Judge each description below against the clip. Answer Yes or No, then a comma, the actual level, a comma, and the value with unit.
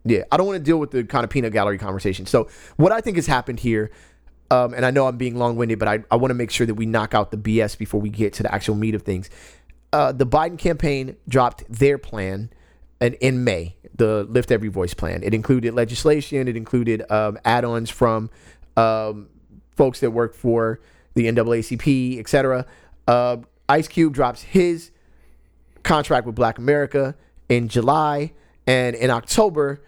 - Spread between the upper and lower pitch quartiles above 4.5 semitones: No, average, 3.8 semitones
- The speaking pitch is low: Yes, low, 120 Hz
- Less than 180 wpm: No, average, 195 wpm